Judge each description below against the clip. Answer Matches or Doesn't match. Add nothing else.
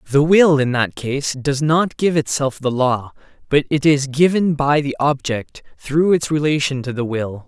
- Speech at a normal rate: Matches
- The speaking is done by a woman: Doesn't match